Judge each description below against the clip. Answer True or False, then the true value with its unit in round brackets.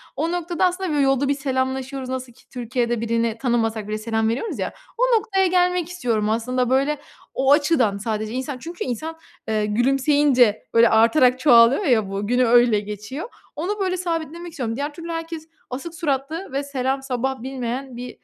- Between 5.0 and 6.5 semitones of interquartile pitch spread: True (5.3 semitones)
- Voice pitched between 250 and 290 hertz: True (260 Hz)